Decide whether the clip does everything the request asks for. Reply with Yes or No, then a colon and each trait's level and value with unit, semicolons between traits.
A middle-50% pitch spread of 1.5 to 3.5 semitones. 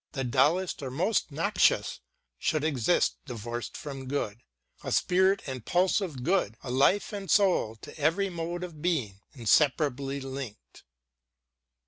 No: wide, 5.6 semitones